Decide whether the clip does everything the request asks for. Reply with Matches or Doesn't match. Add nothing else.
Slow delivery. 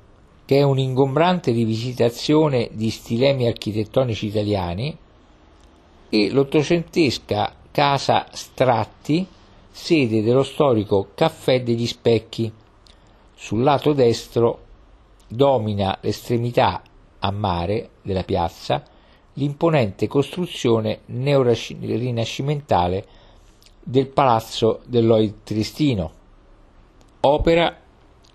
Matches